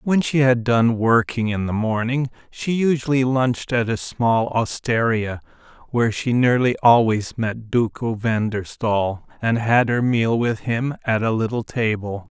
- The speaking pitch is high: No, low, 120 Hz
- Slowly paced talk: No, average, 165 wpm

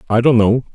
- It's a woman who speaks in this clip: No, male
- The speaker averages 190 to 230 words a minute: No, fast, 240 wpm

